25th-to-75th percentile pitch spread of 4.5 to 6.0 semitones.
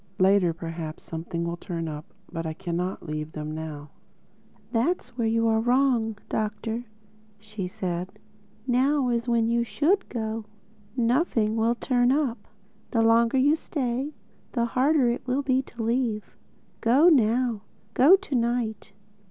Yes: average, 5.1 semitones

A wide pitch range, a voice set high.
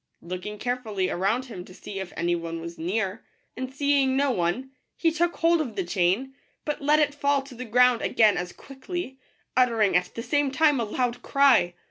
Yes: wide, 6.7 semitones; high, 245 Hz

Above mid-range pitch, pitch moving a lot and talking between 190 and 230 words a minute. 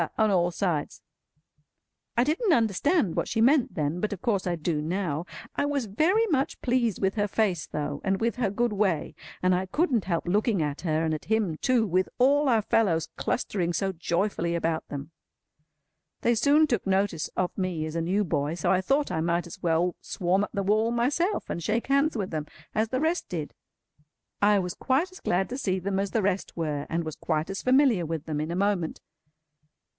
Yes: high, 195 Hz; wide, 5.7 semitones; average, 200 wpm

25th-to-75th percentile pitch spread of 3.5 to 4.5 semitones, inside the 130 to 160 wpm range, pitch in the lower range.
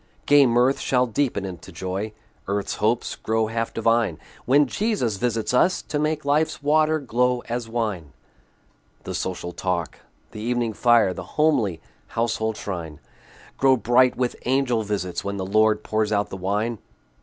Yes: average, 3.8 semitones; average, 155 wpm; low, 115 Hz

